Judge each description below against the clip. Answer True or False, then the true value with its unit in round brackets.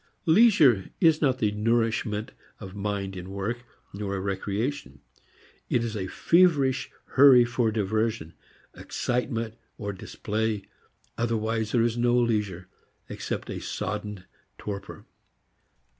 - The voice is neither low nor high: False (110 Hz)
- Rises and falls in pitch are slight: False (3.3 semitones)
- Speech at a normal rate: False (115 wpm)